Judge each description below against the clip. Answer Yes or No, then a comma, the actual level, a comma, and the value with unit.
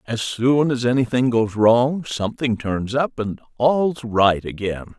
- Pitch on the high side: No, low, 120 Hz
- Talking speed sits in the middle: Yes, average, 155 wpm